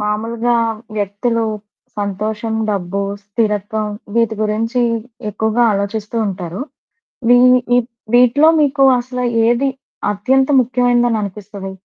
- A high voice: Yes, high, 220 Hz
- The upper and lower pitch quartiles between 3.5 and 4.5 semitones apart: No, average, 2.9 semitones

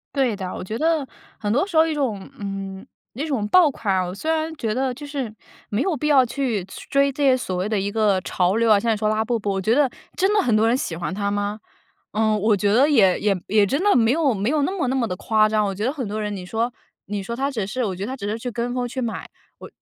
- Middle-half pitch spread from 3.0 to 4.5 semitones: No, average, 4.9 semitones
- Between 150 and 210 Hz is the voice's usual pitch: No, high, 225 Hz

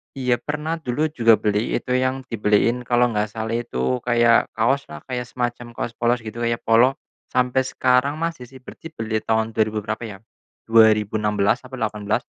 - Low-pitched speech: Yes, low, 120 Hz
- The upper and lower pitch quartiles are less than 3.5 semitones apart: Yes, average, 2.7 semitones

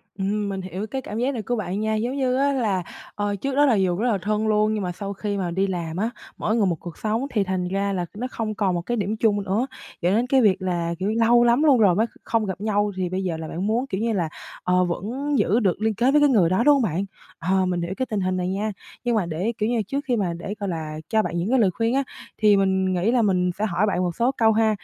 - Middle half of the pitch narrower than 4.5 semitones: Yes, average, 3.7 semitones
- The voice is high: Yes, high, 205 Hz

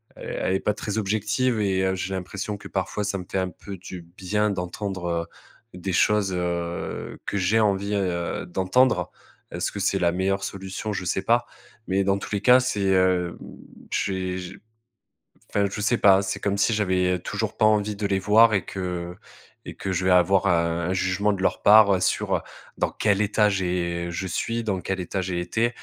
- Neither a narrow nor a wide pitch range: No, narrow, 2.2 semitones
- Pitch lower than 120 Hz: Yes, very low, 95 Hz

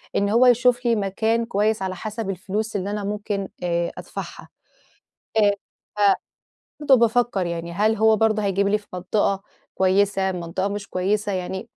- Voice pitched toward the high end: Yes, high, 205 Hz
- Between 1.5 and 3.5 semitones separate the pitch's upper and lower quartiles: Yes, narrow, 2.5 semitones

